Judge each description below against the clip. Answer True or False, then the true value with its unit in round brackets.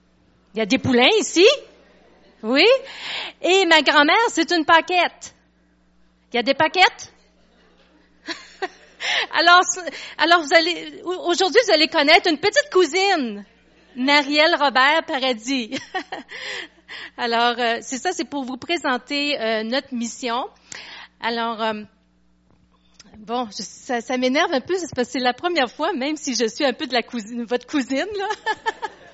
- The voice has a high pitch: True (280 Hz)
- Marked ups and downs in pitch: True (6.5 semitones)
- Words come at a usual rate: False (140 wpm)